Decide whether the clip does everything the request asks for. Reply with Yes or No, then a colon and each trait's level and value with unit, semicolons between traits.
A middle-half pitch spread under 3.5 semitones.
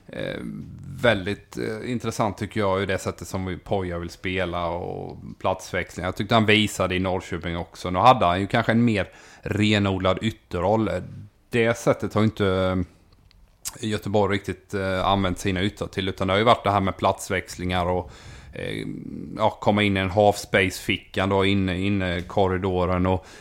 Yes: narrow, 2.4 semitones